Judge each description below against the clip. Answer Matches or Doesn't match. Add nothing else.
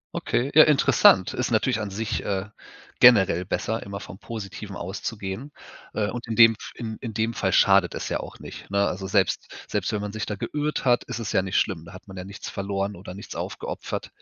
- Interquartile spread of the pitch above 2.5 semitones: Matches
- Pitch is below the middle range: Matches